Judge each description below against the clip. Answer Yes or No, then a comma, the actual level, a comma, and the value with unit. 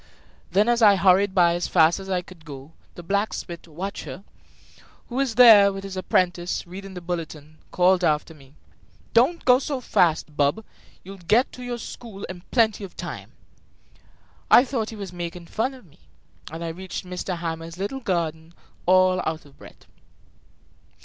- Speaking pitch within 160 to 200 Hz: Yes, medium, 185 Hz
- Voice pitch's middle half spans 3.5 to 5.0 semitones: Yes, average, 3.8 semitones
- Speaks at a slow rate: No, average, 165 wpm